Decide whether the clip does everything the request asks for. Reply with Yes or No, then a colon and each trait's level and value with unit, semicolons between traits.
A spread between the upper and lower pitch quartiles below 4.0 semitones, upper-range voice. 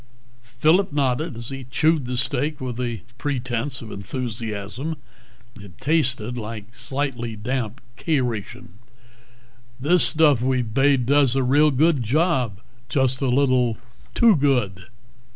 No: average, 3.5 semitones; low, 125 Hz